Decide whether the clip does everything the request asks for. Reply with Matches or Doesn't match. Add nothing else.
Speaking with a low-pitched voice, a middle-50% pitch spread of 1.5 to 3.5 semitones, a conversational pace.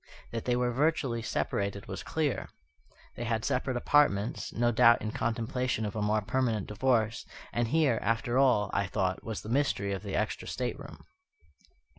Matches